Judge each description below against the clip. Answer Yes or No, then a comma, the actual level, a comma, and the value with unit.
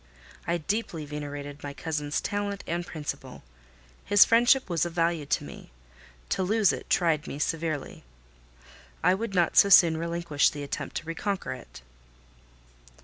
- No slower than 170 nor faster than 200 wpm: No, average, 145 wpm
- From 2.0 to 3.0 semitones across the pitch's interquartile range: No, average, 4.5 semitones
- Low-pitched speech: No, medium, 170 Hz